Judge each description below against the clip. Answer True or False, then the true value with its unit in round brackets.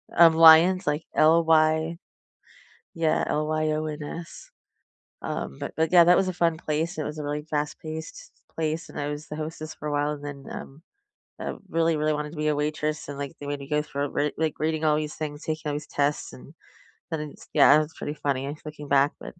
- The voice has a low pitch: False (155 Hz)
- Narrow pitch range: True (1.4 semitones)